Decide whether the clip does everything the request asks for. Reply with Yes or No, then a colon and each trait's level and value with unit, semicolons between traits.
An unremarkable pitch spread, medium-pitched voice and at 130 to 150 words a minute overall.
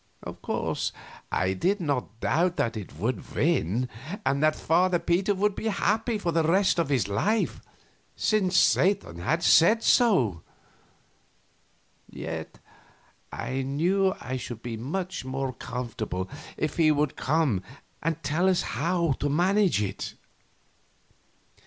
No: wide, 6.8 semitones; medium, 160 Hz; slow, 135 wpm